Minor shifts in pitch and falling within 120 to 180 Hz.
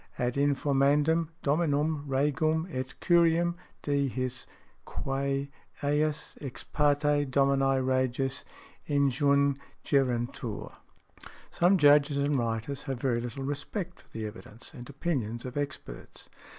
Yes: narrow, 2.1 semitones; medium, 140 Hz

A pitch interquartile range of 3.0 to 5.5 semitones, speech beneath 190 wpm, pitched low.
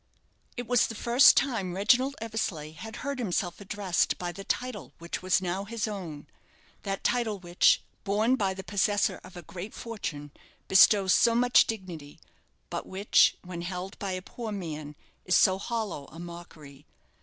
No: average, 4.2 semitones; average, 165 wpm; high, 195 Hz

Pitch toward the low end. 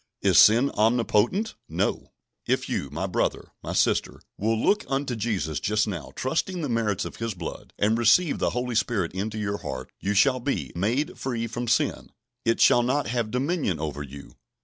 Yes: low, 115 Hz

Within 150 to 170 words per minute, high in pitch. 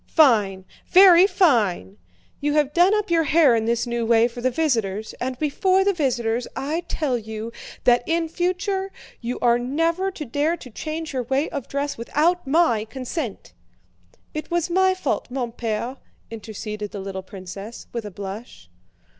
Yes: average, 165 wpm; very high, 255 Hz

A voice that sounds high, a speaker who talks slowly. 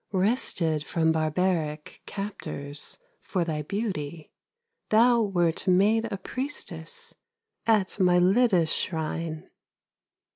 No: medium, 180 Hz; slow, 85 wpm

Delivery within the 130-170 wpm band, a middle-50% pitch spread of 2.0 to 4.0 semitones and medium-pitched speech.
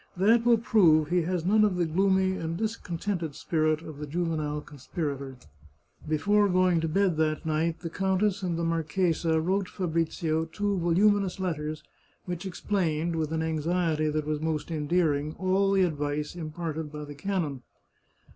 Yes: average, 155 wpm; average, 3.3 semitones; medium, 165 Hz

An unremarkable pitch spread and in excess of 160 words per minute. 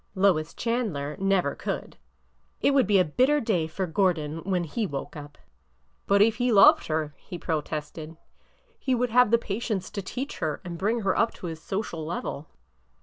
No: wide, 5.9 semitones; average, 180 wpm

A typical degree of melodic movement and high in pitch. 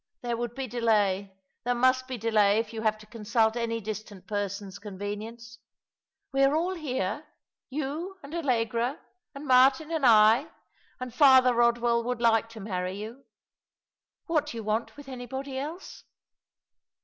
Yes: average, 3.6 semitones; high, 235 Hz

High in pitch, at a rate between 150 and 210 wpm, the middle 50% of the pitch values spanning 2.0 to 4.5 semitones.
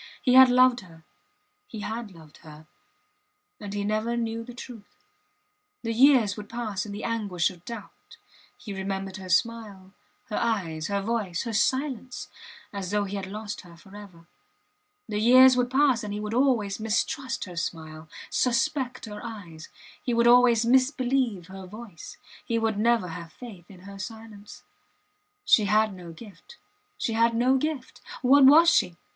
Yes: high, 215 Hz; average, 165 wpm; average, 3.9 semitones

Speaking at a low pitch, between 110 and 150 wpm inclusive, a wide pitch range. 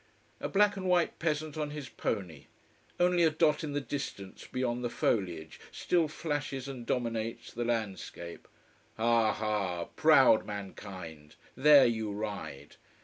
Yes: low, 120 Hz; average, 140 wpm; wide, 6.6 semitones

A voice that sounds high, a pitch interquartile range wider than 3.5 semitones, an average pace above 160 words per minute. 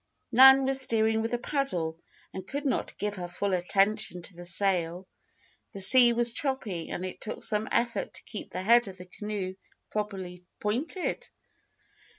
Yes: high, 210 Hz; average, 4.5 semitones; average, 170 wpm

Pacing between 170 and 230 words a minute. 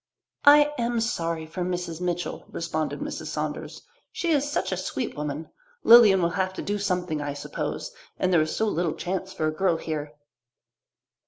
Yes: average, 175 wpm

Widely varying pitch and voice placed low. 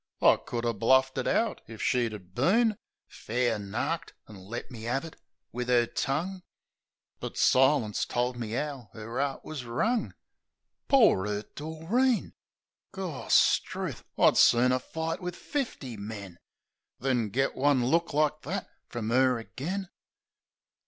Yes: wide, 5.7 semitones; low, 130 Hz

